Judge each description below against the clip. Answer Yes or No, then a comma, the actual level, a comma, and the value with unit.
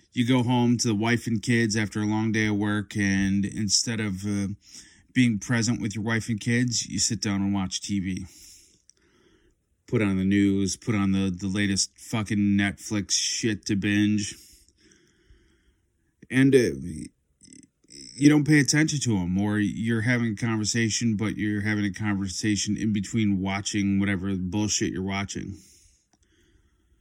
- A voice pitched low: Yes, low, 105 Hz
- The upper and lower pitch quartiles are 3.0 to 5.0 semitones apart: No, narrow, 2.6 semitones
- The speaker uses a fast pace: No, average, 155 wpm